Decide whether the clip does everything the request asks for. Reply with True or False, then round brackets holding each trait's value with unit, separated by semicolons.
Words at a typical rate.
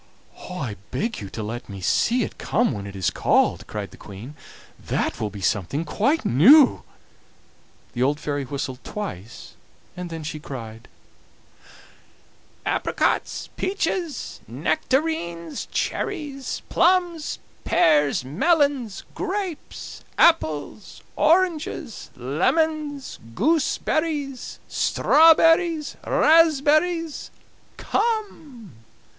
False (95 wpm)